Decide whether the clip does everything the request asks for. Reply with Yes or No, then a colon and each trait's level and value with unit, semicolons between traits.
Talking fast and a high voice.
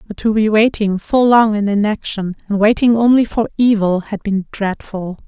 No: average, 180 wpm; high, 210 Hz